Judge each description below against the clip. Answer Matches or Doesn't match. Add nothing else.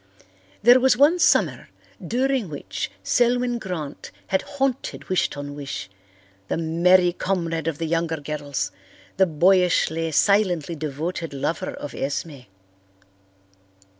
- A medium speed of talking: Doesn't match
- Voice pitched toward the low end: Doesn't match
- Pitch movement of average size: Matches